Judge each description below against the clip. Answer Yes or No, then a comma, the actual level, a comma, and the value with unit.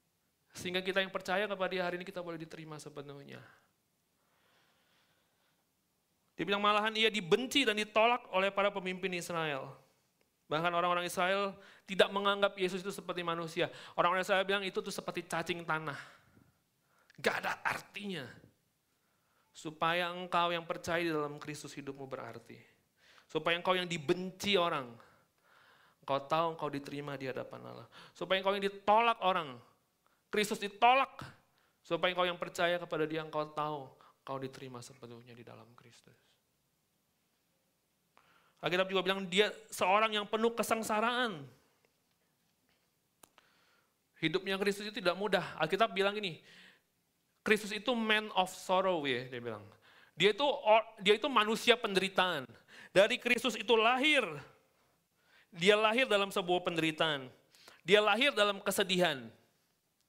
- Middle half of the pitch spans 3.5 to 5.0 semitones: Yes, average, 4.6 semitones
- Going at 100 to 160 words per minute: Yes, average, 130 wpm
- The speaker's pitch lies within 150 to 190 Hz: Yes, medium, 185 Hz